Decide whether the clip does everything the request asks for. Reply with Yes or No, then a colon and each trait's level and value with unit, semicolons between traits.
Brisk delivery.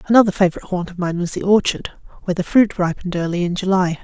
Yes: fast, 225 wpm